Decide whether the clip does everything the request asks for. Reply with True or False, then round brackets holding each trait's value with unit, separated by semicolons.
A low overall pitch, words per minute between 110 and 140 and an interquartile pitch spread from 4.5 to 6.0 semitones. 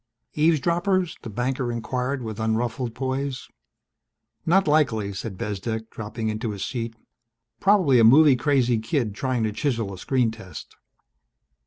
False (120 Hz; 135 wpm; 3.9 semitones)